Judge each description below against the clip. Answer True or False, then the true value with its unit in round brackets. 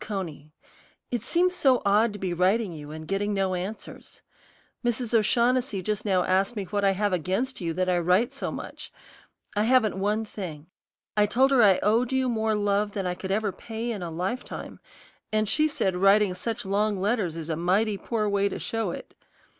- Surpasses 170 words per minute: True (200 wpm)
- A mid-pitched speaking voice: False (205 Hz)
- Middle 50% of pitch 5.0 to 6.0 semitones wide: False (3.3 semitones)